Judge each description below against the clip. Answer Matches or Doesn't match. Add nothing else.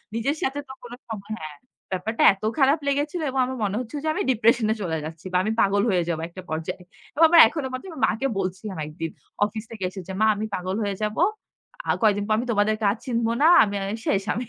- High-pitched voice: Matches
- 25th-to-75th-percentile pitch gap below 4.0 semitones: Doesn't match